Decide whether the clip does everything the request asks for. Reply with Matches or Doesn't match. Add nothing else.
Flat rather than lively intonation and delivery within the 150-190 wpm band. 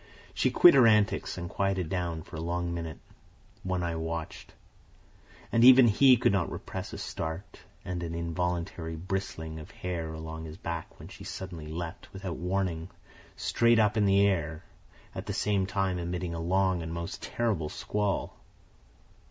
Doesn't match